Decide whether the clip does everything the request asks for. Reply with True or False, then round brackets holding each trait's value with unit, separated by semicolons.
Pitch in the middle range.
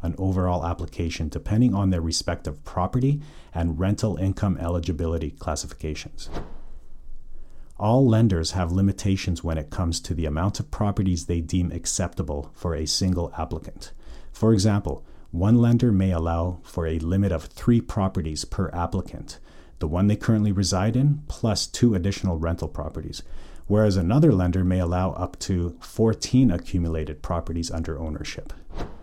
False (90 Hz)